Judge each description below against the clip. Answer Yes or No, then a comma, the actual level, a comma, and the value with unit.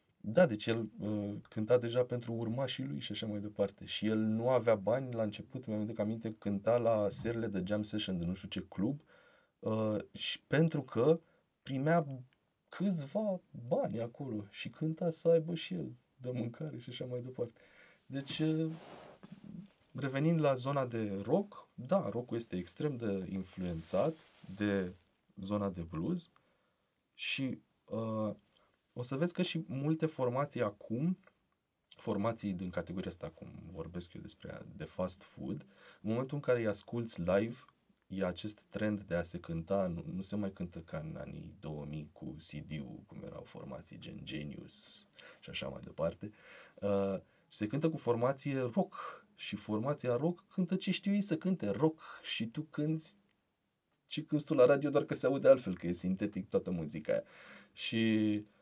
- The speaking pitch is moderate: No, low, 115 Hz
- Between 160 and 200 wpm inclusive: Yes, average, 165 wpm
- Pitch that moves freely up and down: Yes, wide, 6.8 semitones